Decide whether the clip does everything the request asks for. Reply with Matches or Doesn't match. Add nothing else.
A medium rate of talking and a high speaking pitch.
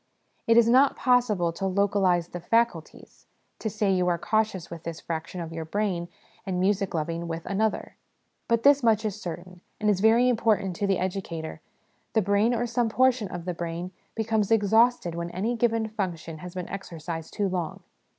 Matches